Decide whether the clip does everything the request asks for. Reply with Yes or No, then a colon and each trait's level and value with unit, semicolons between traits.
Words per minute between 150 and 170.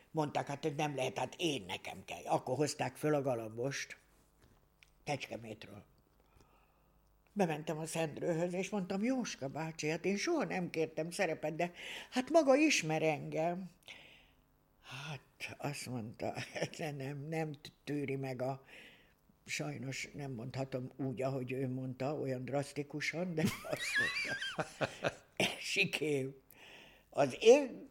No: average, 120 wpm